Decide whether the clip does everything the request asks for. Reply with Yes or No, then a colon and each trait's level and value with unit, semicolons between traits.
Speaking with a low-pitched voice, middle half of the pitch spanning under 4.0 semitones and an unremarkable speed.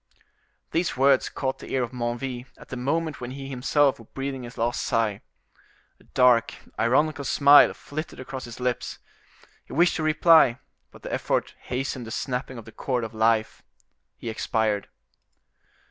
Yes: low, 130 Hz; average, 2.9 semitones; average, 160 wpm